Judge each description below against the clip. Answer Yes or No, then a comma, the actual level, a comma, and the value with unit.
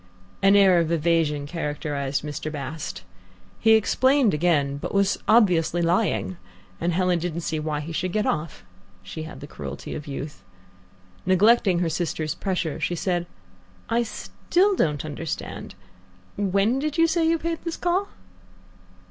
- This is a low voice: No, medium, 175 Hz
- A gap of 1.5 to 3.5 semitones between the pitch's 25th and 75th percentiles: No, wide, 5.5 semitones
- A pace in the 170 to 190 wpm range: No, average, 150 wpm